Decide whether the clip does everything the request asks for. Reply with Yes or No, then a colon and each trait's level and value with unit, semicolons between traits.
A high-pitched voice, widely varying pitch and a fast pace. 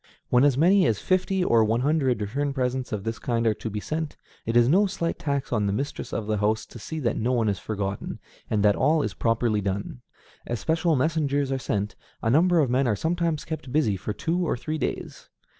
No: low, 125 Hz; wide, 6.3 semitones; fast, 225 wpm